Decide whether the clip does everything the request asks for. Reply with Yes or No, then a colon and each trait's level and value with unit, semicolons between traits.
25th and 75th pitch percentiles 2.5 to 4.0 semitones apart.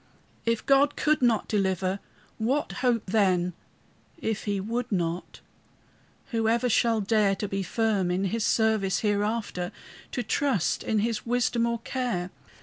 Yes: average, 3.2 semitones